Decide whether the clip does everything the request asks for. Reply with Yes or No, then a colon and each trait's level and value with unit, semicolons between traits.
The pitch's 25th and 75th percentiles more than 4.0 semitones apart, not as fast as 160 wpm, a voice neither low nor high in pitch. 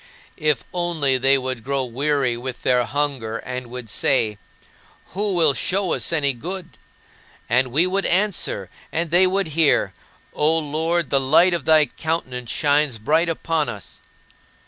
Yes: average, 4.7 semitones; average, 150 wpm; medium, 145 Hz